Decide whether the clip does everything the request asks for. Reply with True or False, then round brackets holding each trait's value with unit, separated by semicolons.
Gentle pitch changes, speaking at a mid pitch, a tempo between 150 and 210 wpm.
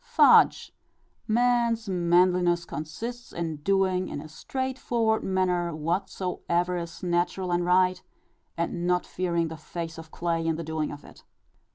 False (2.1 semitones; 175 Hz; 140 wpm)